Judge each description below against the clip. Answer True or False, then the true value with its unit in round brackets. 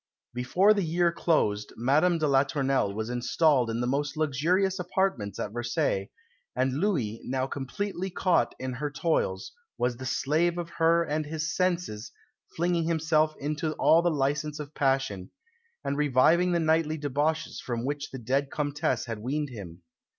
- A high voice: False (145 Hz)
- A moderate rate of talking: True (160 wpm)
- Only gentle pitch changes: False (4.6 semitones)